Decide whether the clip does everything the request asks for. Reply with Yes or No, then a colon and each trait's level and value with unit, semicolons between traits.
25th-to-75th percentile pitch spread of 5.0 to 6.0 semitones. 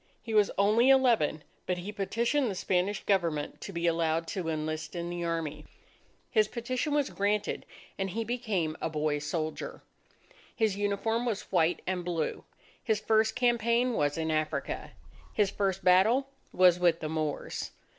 Yes: wide, 5.4 semitones